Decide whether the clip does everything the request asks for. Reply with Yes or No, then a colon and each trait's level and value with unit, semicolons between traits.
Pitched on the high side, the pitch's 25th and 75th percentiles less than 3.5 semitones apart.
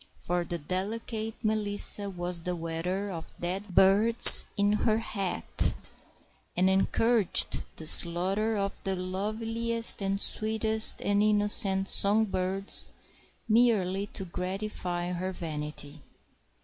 Yes: high, 195 Hz; average, 3.1 semitones